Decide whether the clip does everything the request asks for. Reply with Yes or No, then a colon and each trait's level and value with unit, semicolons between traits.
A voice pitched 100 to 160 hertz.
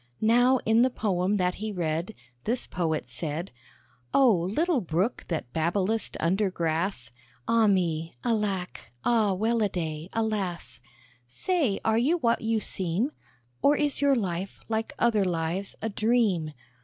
No: high, 200 Hz